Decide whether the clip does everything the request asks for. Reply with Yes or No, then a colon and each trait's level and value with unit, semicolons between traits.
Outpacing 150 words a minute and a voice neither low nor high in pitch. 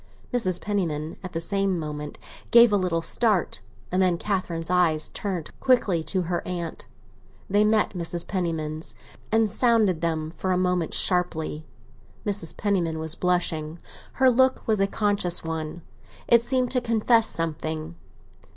No: average, 145 wpm; medium, 180 Hz